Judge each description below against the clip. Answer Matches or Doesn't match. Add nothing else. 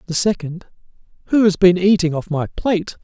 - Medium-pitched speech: Matches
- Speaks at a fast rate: Doesn't match